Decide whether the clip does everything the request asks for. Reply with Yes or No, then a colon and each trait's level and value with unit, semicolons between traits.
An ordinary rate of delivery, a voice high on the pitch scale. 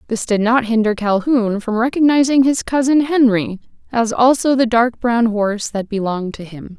Yes: average, 175 wpm; high, 235 Hz